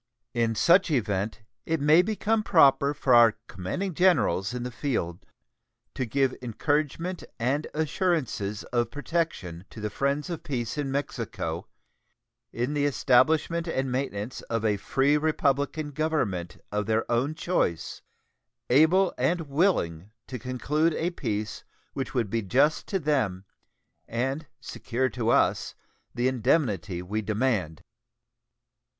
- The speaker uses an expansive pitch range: Yes, wide, 5.9 semitones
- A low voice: Yes, low, 130 Hz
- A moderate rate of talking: No, slow, 130 wpm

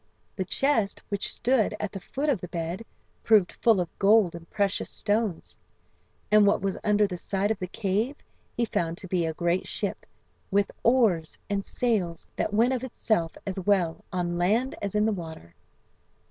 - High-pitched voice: Yes, high, 200 Hz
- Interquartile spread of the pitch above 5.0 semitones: No, average, 3.8 semitones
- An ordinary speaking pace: Yes, average, 180 wpm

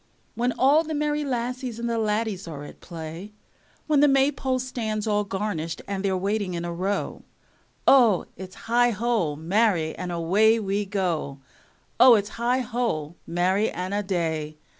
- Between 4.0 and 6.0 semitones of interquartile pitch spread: Yes, average, 5.3 semitones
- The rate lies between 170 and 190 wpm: No, average, 155 wpm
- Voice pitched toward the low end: No, high, 205 Hz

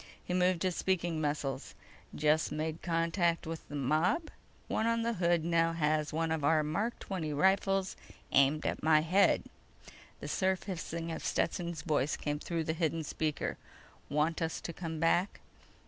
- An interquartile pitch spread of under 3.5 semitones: Yes, average, 2.7 semitones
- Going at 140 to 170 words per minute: Yes, average, 165 wpm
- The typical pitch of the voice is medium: Yes, medium, 165 Hz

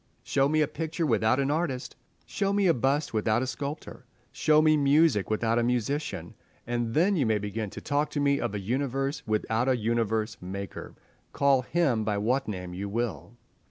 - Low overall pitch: Yes, low, 125 Hz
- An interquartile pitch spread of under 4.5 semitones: No, average, 5.0 semitones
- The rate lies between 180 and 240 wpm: Yes, average, 190 wpm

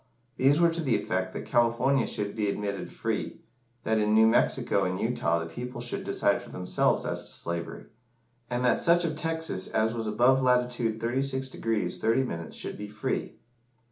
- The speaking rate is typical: Yes, average, 170 wpm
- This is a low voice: Yes, low, 115 Hz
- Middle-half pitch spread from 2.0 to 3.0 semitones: No, average, 4.0 semitones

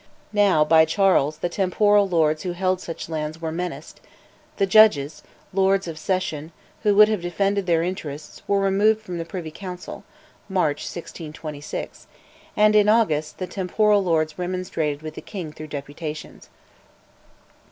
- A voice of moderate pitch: Yes, medium, 175 Hz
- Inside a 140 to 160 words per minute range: Yes, average, 145 wpm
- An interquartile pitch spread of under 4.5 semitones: Yes, average, 4.0 semitones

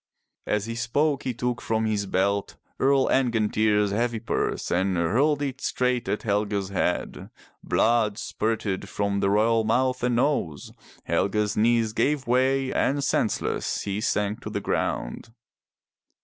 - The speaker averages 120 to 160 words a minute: Yes, average, 145 wpm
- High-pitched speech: No, low, 110 Hz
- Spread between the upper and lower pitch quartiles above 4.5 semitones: No, average, 3.8 semitones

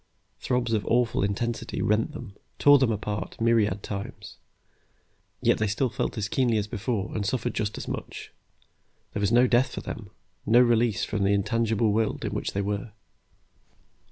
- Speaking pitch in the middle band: No, low, 110 Hz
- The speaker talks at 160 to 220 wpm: Yes, average, 170 wpm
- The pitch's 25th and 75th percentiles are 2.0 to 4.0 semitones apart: Yes, narrow, 2.6 semitones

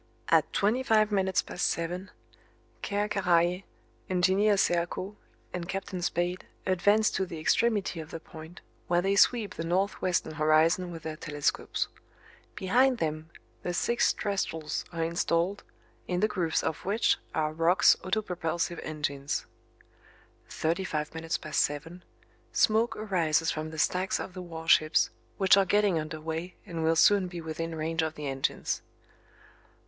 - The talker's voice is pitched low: No, medium, 175 Hz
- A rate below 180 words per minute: Yes, average, 145 wpm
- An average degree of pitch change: Yes, average, 3.2 semitones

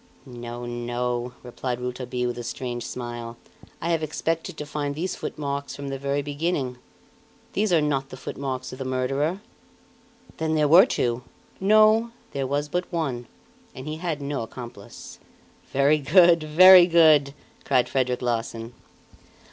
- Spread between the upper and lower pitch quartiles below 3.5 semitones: No, average, 4.2 semitones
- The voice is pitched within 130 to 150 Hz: Yes, medium, 140 Hz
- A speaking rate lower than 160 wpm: Yes, average, 150 wpm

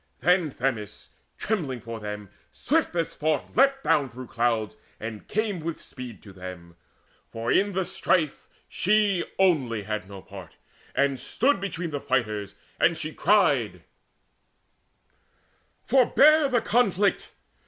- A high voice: No, medium, 145 Hz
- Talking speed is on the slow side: Yes, slow, 130 wpm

